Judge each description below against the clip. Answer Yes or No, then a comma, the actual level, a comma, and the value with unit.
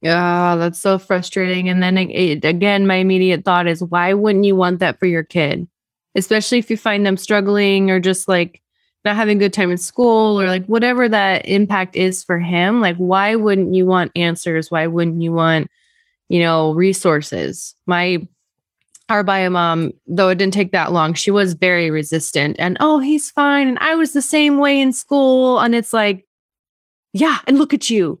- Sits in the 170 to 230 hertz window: Yes, high, 190 Hz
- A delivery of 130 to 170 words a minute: No, average, 195 wpm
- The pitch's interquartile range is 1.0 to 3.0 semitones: No, average, 3.7 semitones